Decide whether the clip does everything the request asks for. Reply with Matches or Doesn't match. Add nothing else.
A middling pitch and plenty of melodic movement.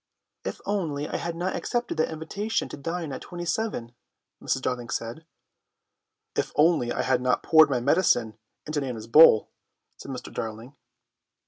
Matches